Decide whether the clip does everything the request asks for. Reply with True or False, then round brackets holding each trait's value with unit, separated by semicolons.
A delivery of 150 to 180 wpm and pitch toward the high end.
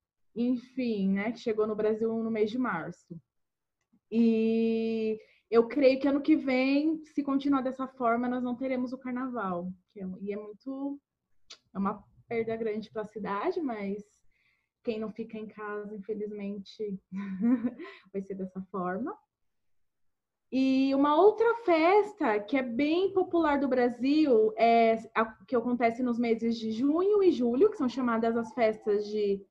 True (155 wpm; 230 Hz)